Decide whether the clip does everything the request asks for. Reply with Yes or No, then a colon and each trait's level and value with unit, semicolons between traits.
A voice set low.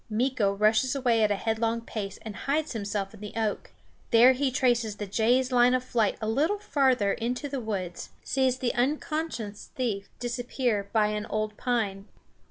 No: high, 230 Hz